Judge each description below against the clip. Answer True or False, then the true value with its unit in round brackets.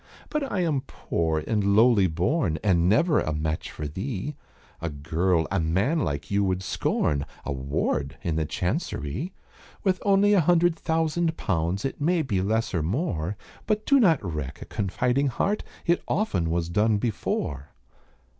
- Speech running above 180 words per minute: False (165 wpm)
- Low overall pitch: True (100 Hz)